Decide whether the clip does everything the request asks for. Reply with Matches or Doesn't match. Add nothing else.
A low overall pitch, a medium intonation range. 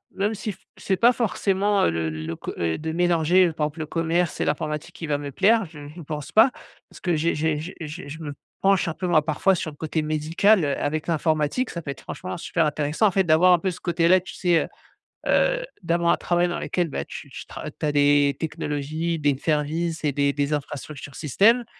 Doesn't match